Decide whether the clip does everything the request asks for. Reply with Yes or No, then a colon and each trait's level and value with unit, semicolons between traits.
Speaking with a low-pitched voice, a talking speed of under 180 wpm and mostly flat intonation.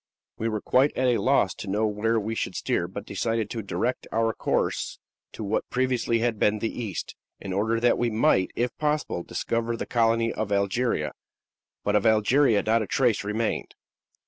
No: low, 115 Hz; average, 185 wpm; narrow, 2.3 semitones